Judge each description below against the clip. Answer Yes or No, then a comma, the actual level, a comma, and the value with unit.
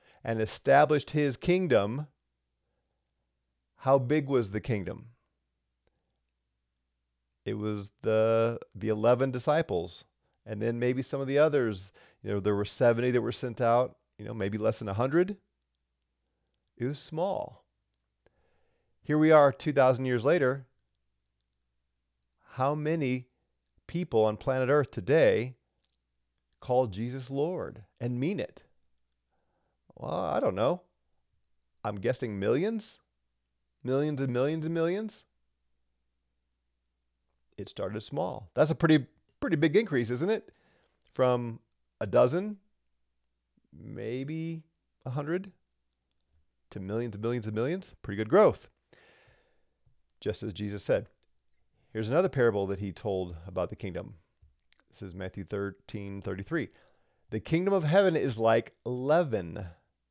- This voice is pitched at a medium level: No, low, 110 Hz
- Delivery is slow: Yes, slow, 120 wpm